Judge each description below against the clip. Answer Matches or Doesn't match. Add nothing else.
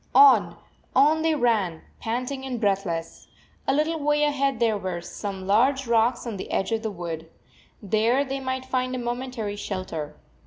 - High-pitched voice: Matches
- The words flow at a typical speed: Matches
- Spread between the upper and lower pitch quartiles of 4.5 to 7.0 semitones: Matches